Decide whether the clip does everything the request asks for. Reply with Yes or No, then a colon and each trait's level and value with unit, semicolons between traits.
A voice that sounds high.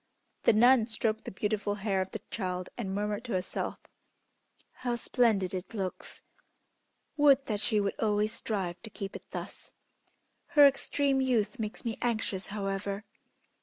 Yes: high, 215 Hz